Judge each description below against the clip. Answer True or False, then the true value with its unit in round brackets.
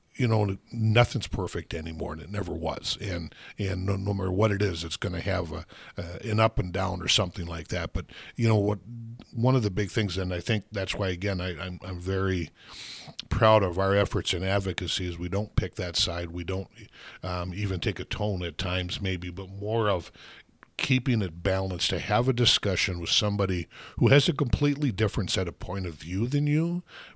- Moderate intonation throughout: True (3.4 semitones)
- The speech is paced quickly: True (210 wpm)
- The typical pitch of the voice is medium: False (100 Hz)